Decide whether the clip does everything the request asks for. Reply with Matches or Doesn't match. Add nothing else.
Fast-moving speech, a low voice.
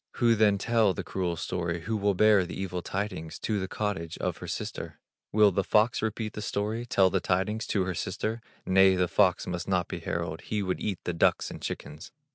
Matches